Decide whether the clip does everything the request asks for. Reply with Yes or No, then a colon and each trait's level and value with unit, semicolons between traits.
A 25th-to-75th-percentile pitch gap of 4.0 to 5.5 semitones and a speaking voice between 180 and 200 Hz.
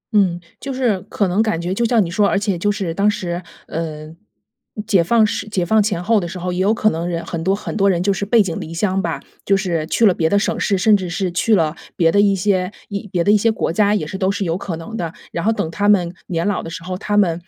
No: average, 3.2 semitones; high, 190 Hz